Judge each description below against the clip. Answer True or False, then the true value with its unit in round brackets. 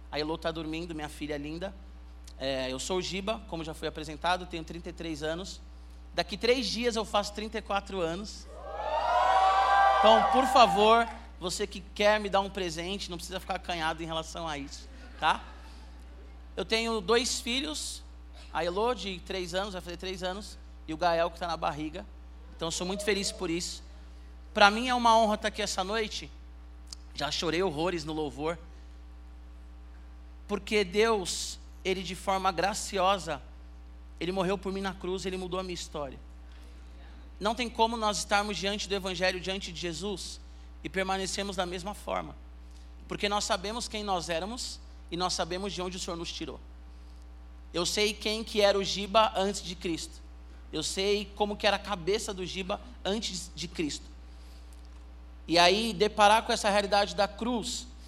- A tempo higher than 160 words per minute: True (170 wpm)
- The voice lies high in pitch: False (180 Hz)